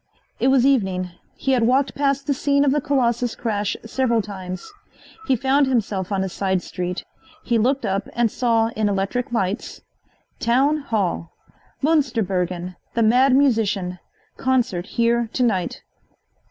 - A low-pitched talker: No, high, 230 Hz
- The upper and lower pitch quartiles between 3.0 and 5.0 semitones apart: No, wide, 5.4 semitones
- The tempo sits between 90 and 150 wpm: Yes, average, 145 wpm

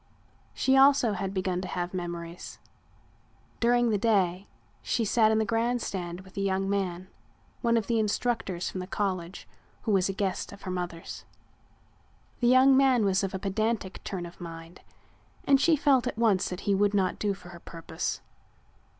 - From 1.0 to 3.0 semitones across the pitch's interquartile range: No, average, 4.0 semitones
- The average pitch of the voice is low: No, high, 195 Hz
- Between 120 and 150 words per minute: No, average, 175 wpm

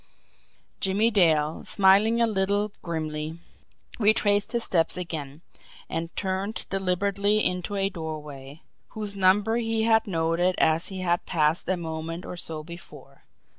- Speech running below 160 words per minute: Yes, slow, 135 wpm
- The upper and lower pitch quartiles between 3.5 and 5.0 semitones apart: Yes, average, 4.0 semitones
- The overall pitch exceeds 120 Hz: Yes, medium, 185 Hz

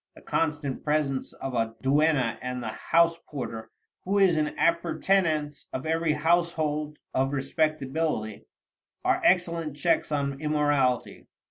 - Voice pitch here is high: No, medium, 150 Hz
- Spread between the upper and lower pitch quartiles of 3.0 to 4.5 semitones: Yes, average, 3.4 semitones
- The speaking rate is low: Yes, slow, 125 wpm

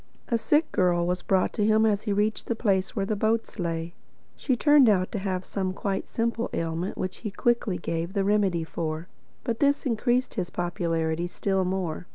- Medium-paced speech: Yes, average, 195 wpm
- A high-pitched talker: Yes, high, 195 Hz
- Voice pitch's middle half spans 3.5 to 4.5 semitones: Yes, average, 4.0 semitones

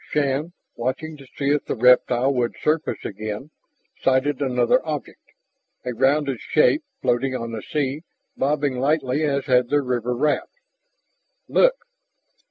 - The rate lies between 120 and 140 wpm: Yes, slow, 135 wpm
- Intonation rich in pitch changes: No, average, 3.0 semitones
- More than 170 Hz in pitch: No, low, 135 Hz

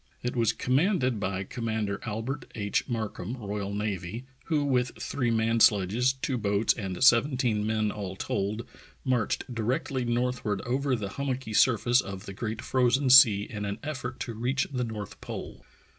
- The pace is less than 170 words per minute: Yes, average, 160 wpm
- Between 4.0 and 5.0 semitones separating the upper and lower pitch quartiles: No, average, 3.6 semitones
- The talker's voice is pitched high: No, low, 115 Hz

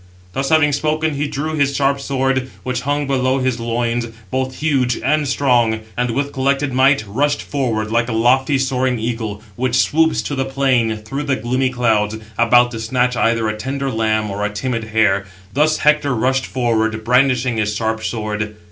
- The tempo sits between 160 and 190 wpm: Yes, average, 180 wpm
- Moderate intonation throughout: Yes, average, 3.5 semitones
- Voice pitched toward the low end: Yes, low, 125 Hz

